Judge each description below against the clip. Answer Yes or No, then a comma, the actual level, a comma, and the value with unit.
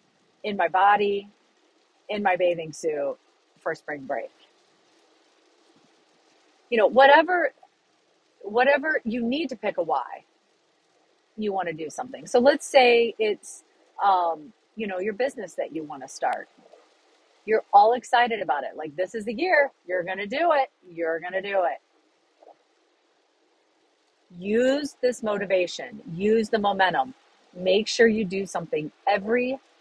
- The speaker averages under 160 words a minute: Yes, average, 140 wpm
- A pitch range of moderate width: No, wide, 8.3 semitones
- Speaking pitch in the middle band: No, high, 235 Hz